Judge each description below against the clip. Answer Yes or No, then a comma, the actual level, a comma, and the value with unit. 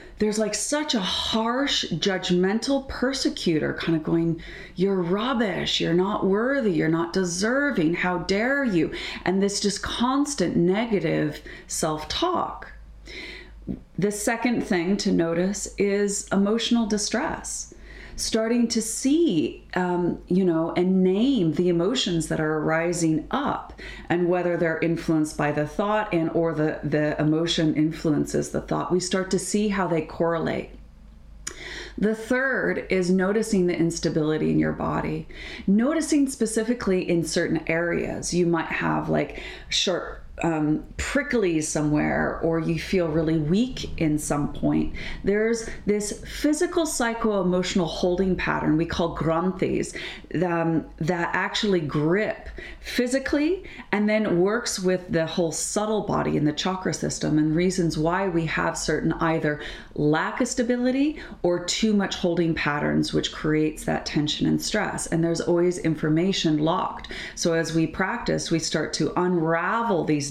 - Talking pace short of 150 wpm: Yes, average, 140 wpm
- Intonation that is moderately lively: Yes, average, 4.9 semitones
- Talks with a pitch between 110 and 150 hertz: No, medium, 180 Hz